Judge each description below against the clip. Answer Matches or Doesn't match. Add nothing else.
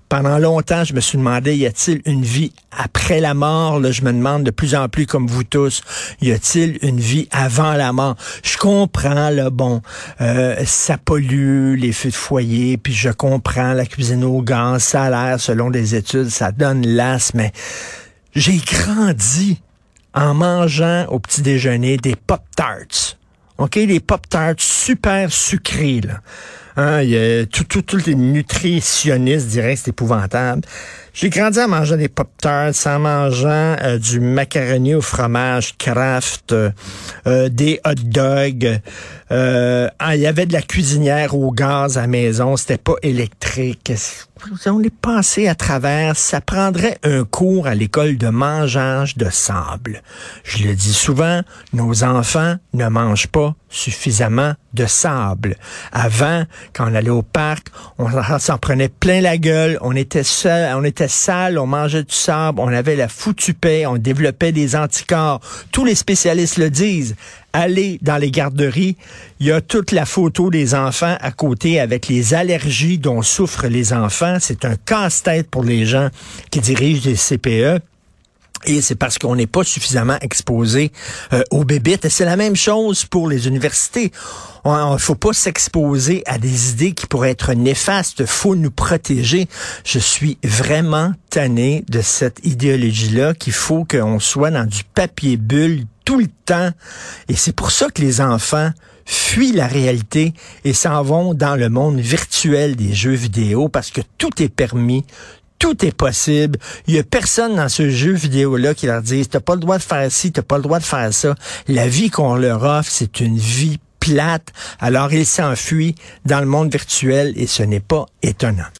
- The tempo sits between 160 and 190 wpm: Matches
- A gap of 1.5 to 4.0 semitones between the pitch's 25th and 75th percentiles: Doesn't match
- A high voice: Doesn't match